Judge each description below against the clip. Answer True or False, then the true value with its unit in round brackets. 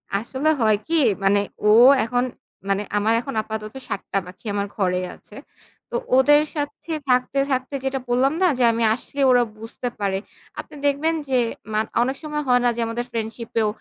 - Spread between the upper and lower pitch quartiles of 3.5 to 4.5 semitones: True (4.0 semitones)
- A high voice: True (245 Hz)